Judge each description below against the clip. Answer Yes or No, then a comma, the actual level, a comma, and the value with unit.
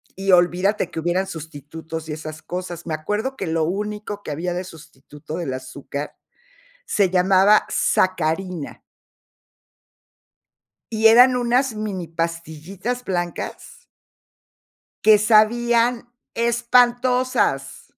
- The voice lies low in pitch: No, medium, 185 Hz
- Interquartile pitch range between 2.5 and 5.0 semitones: No, wide, 5.4 semitones